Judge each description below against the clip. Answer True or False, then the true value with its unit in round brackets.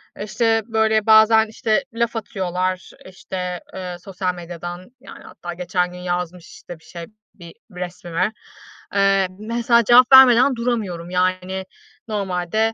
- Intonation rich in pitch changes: False (3.7 semitones)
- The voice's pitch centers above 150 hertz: True (190 Hz)